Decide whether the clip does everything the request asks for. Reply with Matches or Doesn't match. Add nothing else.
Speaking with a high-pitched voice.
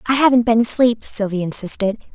Matches